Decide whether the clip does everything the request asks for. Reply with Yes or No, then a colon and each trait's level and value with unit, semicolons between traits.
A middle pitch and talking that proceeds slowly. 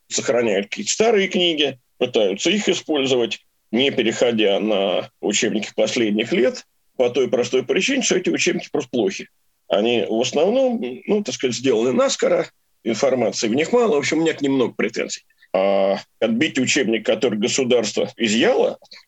No: medium, 175 Hz; average, 145 wpm